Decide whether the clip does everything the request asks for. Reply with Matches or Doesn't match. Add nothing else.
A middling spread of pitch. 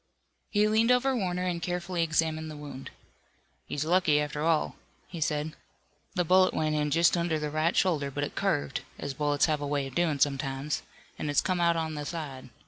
Matches